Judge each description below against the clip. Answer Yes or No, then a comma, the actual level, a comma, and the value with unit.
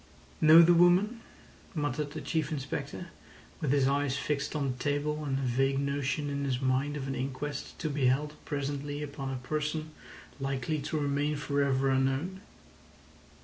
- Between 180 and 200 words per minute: No, average, 165 wpm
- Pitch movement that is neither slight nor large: No, narrow, 1.9 semitones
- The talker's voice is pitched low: No, medium, 145 Hz